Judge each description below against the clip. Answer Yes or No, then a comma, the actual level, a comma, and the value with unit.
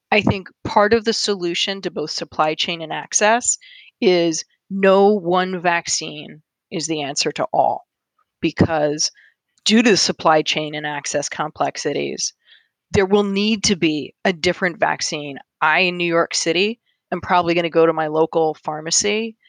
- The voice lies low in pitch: No, medium, 175 Hz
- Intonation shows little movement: No, average, 4.3 semitones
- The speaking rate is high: No, average, 160 wpm